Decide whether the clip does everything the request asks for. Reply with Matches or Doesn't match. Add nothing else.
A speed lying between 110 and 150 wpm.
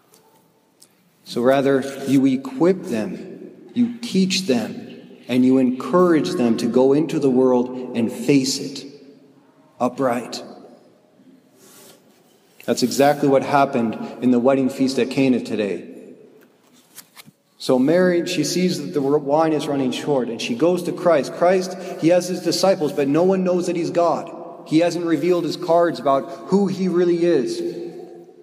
Matches